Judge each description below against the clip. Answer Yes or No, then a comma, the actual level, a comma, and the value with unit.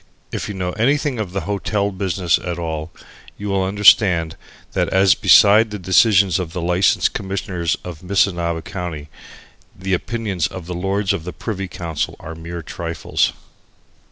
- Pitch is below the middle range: Yes, very low, 95 Hz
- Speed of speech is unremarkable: Yes, average, 155 wpm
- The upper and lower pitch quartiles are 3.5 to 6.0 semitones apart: No, average, 2.8 semitones